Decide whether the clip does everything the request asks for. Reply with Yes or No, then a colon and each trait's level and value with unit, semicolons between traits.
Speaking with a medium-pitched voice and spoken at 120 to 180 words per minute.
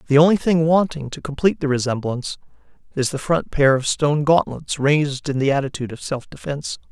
No: medium, 145 Hz; average, 190 wpm